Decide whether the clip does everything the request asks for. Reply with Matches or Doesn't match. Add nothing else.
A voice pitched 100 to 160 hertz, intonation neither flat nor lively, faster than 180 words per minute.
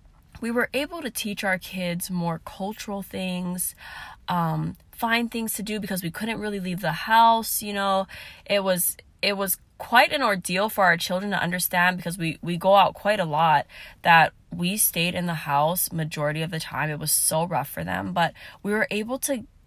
Doesn't match